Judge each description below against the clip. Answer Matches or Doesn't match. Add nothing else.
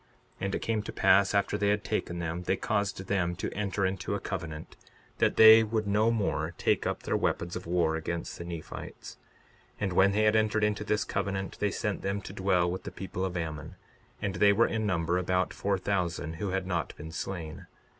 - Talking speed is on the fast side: Matches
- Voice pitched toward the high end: Doesn't match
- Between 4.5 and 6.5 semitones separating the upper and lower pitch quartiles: Doesn't match